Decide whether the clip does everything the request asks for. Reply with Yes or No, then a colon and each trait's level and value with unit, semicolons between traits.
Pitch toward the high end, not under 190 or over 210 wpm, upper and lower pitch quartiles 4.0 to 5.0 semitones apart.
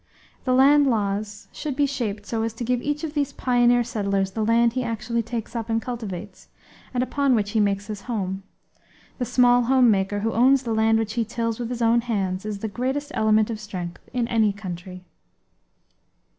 No: high, 225 Hz; average, 195 wpm; average, 3.0 semitones